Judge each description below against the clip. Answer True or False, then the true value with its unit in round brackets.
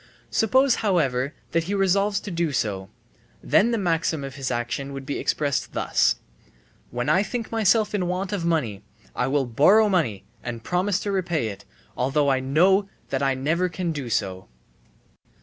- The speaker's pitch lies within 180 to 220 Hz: False (160 Hz)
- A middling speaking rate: True (170 wpm)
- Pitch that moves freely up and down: True (6.8 semitones)